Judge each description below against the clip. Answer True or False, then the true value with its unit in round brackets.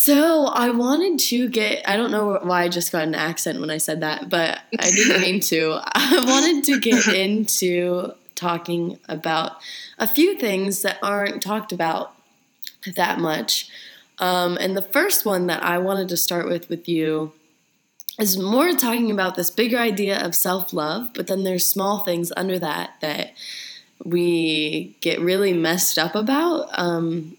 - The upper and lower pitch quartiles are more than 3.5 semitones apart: True (4.2 semitones)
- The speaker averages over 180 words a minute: False (170 wpm)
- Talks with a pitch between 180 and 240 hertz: True (185 Hz)